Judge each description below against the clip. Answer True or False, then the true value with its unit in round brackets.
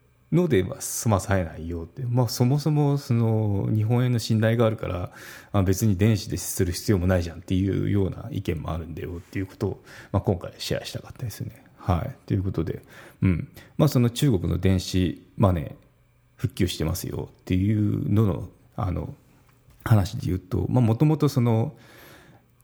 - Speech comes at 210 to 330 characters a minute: False (340 characters per minute)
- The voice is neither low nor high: False (110 Hz)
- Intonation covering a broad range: False (5.0 semitones)